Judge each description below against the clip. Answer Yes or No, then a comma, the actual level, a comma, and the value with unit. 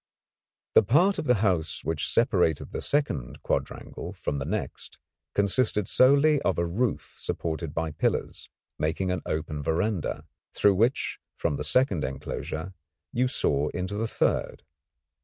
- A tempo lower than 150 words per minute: Yes, average, 140 wpm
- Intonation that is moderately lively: No, wide, 7.0 semitones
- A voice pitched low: Yes, very low, 95 Hz